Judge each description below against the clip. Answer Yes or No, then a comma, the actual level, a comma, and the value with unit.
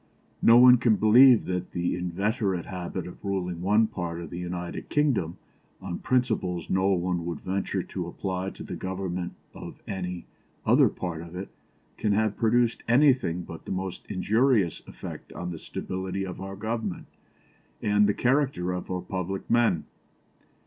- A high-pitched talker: No, very low, 95 Hz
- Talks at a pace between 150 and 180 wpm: Yes, average, 165 wpm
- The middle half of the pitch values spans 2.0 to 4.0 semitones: Yes, average, 3.6 semitones